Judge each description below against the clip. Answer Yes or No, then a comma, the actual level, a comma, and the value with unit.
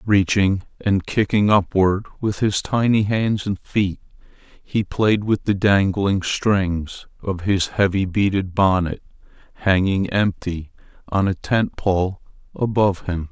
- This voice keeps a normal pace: No, slow, 130 wpm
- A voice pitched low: Yes, very low, 95 Hz